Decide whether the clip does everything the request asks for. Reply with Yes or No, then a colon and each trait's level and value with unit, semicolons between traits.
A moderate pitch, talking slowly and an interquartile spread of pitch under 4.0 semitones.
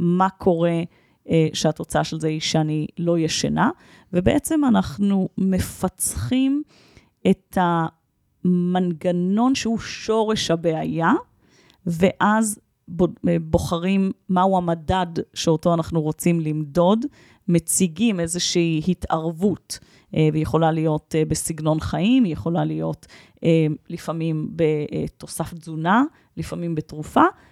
Yes: medium, 170 Hz; slow, 90 wpm; average, 3.3 semitones